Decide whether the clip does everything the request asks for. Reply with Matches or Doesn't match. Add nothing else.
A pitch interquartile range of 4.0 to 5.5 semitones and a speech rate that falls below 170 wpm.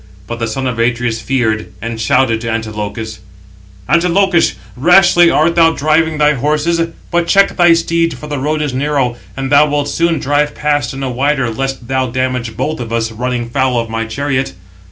Doesn't match